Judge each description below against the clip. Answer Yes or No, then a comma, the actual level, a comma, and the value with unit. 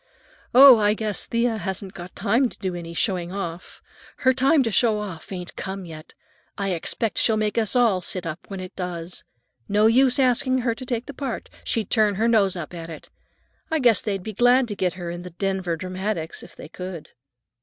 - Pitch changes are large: No, average, 4.5 semitones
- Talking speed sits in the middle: No, fast, 210 wpm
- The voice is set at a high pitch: Yes, high, 200 Hz